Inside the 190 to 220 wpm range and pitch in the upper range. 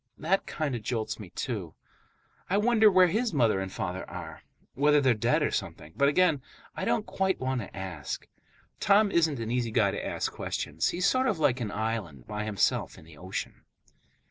No: average, 195 wpm; low, 125 Hz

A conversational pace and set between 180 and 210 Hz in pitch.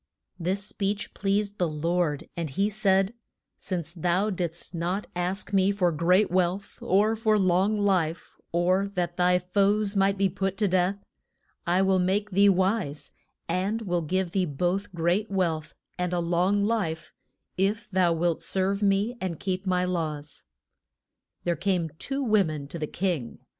Yes: average, 160 wpm; medium, 185 Hz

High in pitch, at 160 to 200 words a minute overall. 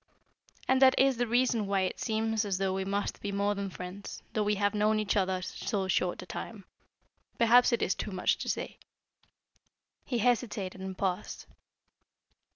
Yes: high, 205 Hz; average, 175 wpm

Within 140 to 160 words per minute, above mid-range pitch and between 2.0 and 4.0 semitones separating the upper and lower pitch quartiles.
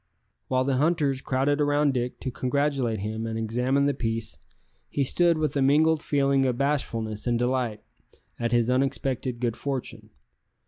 No: average, 155 wpm; low, 130 Hz; average, 3.2 semitones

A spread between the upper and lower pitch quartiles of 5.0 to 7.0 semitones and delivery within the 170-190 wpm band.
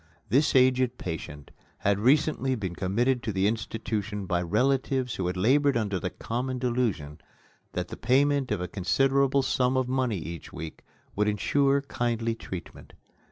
No: wide, 5.6 semitones; average, 155 wpm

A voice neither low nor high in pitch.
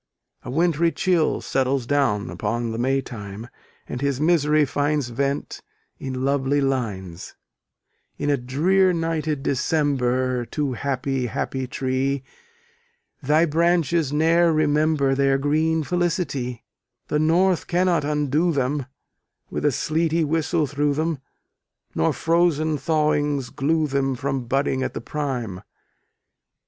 Yes: medium, 145 Hz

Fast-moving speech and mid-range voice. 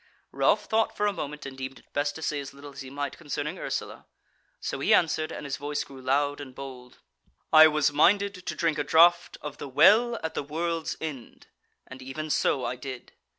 Yes: fast, 210 wpm; medium, 145 Hz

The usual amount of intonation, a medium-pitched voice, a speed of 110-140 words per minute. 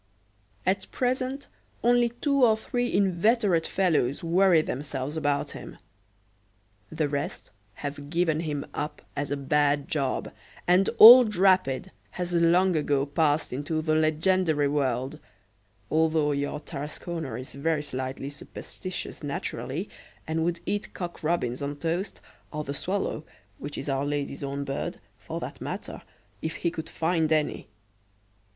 Yes: average, 4.2 semitones; medium, 155 Hz; slow, 135 wpm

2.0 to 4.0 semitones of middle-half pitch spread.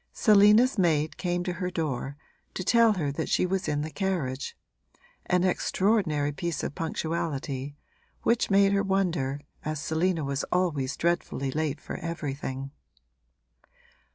No: average, 4.6 semitones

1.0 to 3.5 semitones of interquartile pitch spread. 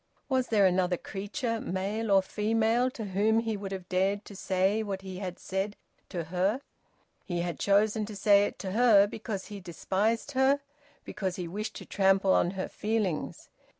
Yes: narrow, 2.6 semitones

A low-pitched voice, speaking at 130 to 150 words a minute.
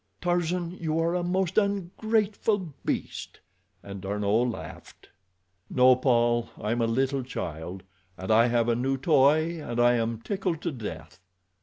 Yes: low, 130 Hz; average, 145 wpm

